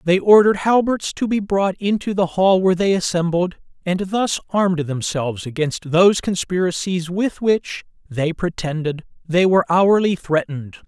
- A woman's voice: No, male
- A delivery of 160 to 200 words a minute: No, average, 150 wpm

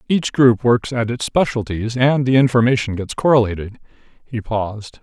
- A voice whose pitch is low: Yes, low, 120 Hz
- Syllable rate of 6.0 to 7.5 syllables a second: No, 5.1 syllables/s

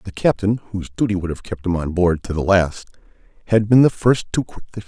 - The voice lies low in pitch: Yes, very low, 95 Hz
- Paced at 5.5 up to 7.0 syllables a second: Yes, 6.0 syllables/s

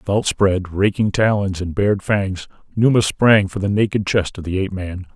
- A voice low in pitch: Yes, low, 100 Hz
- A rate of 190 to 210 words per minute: Yes, average, 200 wpm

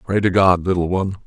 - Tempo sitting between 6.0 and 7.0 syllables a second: Yes, 6.5 syllables/s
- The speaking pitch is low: Yes, very low, 95 Hz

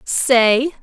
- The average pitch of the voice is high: Yes, very high, 255 Hz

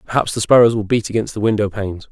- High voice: No, low, 110 Hz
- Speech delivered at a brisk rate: Yes, fast, 225 wpm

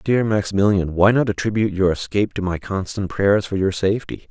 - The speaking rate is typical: Yes, average, 195 wpm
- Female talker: No, male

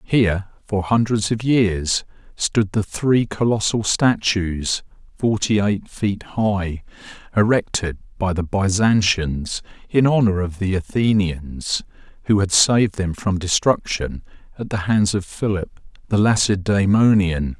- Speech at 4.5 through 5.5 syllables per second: No, 3.9 syllables/s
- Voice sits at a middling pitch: No, low, 100 Hz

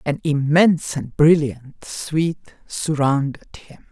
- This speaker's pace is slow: Yes, slow, 105 wpm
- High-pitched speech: No, medium, 150 Hz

